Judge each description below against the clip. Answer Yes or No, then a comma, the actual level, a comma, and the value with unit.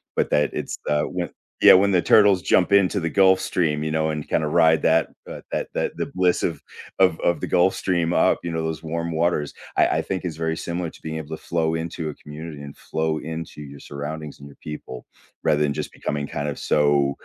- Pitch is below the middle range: Yes, very low, 80 Hz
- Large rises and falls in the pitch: No, average, 2.7 semitones